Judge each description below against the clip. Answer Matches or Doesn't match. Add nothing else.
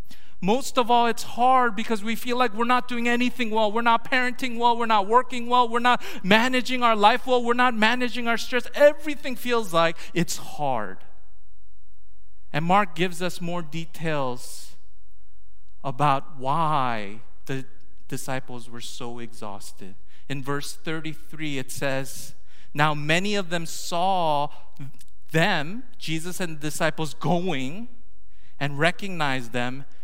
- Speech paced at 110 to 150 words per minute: Matches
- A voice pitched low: Doesn't match